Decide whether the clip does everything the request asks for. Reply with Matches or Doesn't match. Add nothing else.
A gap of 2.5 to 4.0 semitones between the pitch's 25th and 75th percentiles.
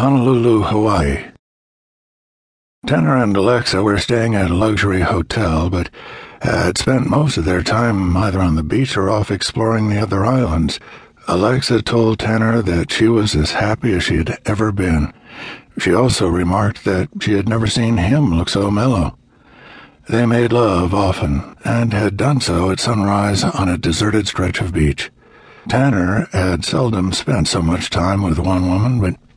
Doesn't match